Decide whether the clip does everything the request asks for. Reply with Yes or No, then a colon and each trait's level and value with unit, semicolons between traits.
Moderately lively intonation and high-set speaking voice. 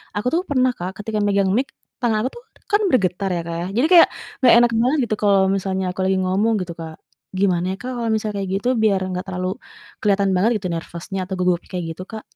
Yes: average, 3.5 semitones; high, 195 Hz